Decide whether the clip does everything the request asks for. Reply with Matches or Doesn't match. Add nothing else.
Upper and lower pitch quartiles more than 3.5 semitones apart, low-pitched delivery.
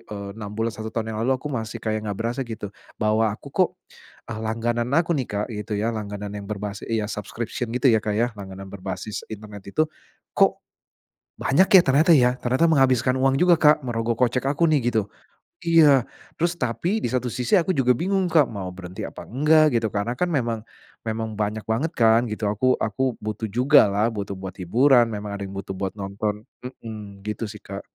Matches